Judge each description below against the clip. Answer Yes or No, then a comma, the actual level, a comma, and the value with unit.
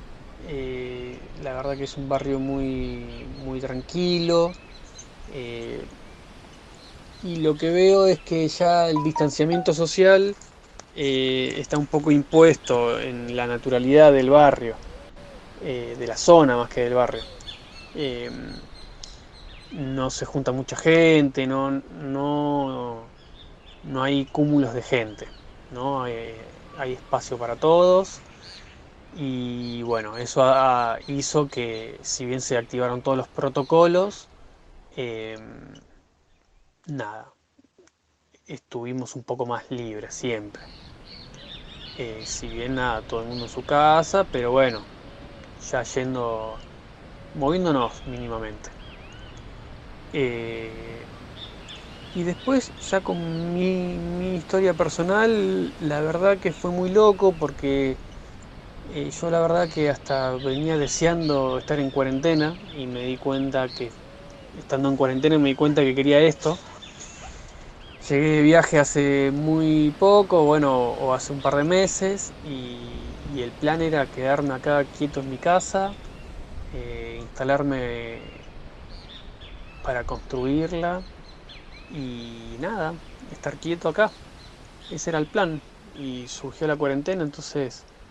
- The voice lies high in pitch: No, low, 135 Hz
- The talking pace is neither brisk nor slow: No, slow, 120 wpm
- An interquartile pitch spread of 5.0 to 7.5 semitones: No, average, 4.4 semitones